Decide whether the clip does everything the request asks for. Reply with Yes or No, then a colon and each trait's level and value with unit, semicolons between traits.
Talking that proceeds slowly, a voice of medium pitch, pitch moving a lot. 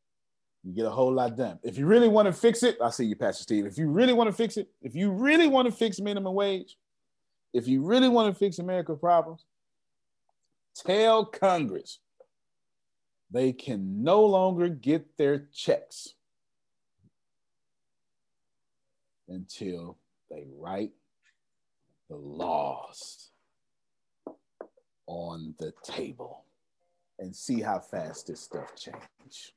Yes: slow, 130 wpm; medium, 175 Hz; wide, 8.9 semitones